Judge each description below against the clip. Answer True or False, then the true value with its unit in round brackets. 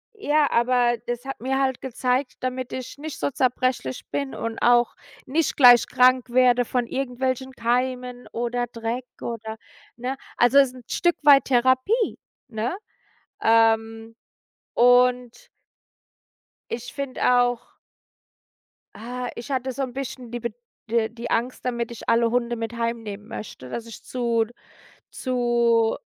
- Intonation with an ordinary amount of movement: False (1.8 semitones)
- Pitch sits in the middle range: False (245 Hz)